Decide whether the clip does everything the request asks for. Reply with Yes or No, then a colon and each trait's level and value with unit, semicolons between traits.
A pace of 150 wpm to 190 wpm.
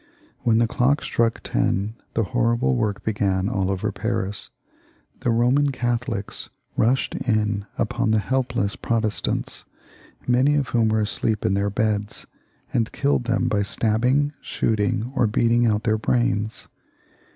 No: average, 140 wpm